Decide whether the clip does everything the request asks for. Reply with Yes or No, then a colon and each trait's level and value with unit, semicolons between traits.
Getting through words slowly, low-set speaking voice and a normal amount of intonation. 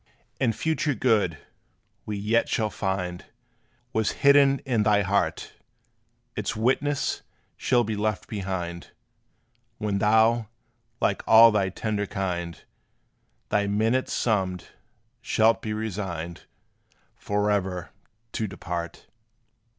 Yes: slow, 105 wpm; low, 105 Hz; average, 3.1 semitones